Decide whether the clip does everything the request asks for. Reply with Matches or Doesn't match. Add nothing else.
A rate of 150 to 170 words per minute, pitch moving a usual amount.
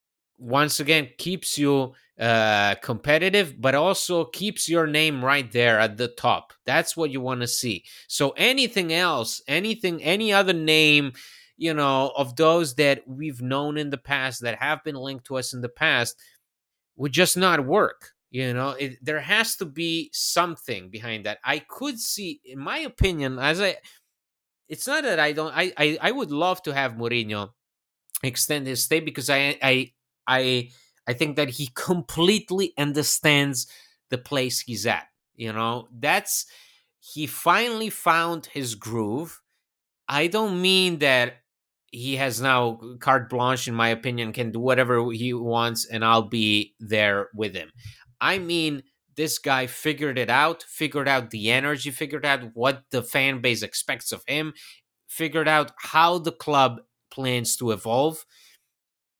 Matches